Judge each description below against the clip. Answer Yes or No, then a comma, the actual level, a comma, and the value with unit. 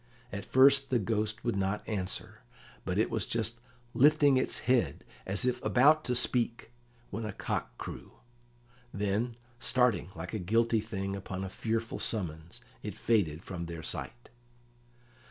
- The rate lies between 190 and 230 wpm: No, average, 150 wpm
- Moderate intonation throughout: Yes, average, 4.2 semitones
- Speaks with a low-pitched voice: Yes, low, 110 Hz